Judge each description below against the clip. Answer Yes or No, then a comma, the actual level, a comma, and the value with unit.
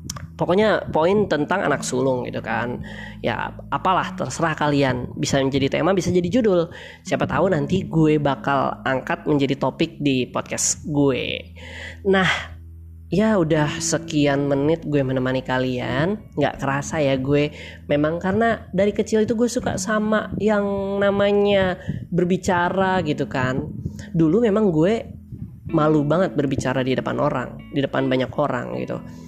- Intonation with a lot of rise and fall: Yes, wide, 5.8 semitones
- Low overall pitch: No, medium, 150 Hz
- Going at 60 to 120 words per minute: No, average, 135 wpm